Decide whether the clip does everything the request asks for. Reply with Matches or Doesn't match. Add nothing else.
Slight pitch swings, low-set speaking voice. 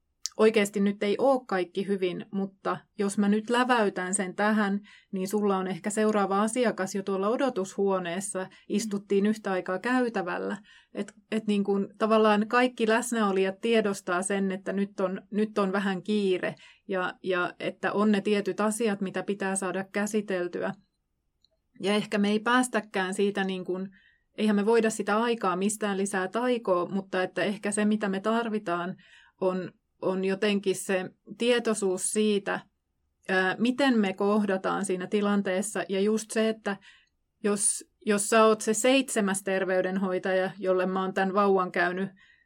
Doesn't match